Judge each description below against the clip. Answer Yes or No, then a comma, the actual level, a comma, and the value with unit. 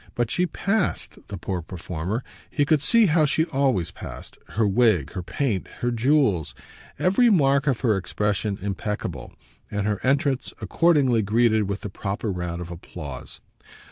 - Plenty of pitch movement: Yes, wide, 6.6 semitones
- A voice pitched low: Yes, low, 110 Hz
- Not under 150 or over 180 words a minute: Yes, average, 155 wpm